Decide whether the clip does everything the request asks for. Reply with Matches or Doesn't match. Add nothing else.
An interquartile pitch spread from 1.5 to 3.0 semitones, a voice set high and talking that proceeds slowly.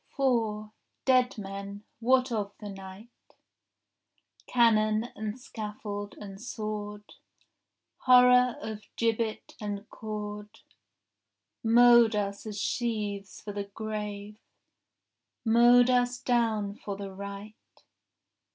Matches